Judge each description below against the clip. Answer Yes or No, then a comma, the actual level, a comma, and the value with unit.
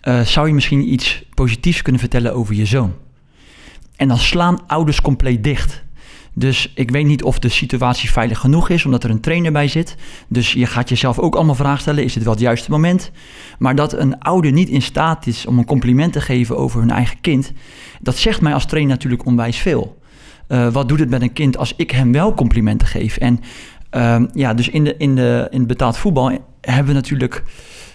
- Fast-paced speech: Yes, fast, 215 wpm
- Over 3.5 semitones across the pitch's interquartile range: No, average, 3.2 semitones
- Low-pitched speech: Yes, low, 130 Hz